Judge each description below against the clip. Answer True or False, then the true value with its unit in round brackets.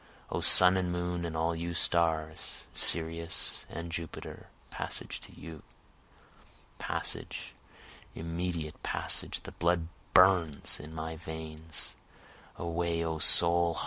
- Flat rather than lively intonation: True (1.2 semitones)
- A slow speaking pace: True (110 wpm)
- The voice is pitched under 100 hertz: True (85 Hz)